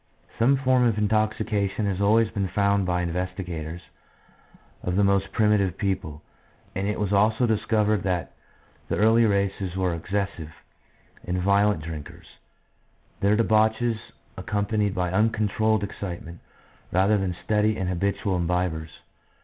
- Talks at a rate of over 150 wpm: No, slow, 135 wpm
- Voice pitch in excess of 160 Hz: No, low, 100 Hz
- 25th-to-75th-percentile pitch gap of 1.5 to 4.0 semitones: Yes, average, 3.0 semitones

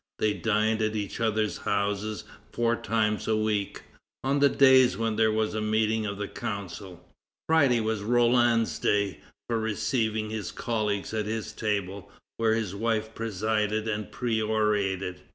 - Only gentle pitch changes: Yes, narrow, 1.5 semitones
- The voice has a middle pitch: No, low, 110 Hz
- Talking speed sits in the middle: Yes, average, 150 wpm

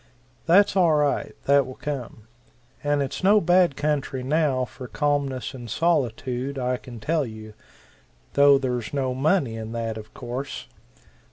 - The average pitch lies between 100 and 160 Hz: Yes, low, 135 Hz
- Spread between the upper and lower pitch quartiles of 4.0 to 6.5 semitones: No, average, 3.1 semitones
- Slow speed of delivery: No, average, 150 wpm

